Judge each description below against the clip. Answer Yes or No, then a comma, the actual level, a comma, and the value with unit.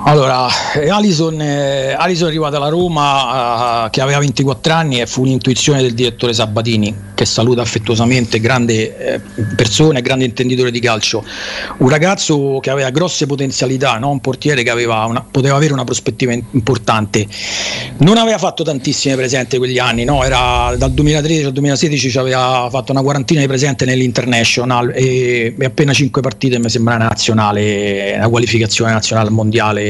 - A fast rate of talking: No, average, 160 wpm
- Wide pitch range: No, average, 3.2 semitones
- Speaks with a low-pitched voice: Yes, low, 130 Hz